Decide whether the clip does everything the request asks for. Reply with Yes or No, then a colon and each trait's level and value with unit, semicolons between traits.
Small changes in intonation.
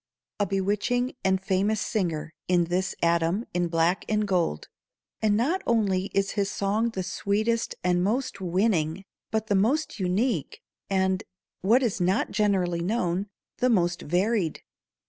No: average, 3.5 semitones